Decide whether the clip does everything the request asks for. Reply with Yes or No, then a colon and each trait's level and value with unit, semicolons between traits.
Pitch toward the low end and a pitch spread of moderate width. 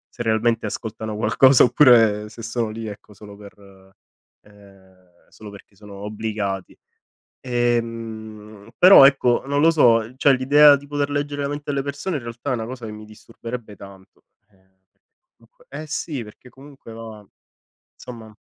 Yes: low, 115 Hz; average, 4.2 semitones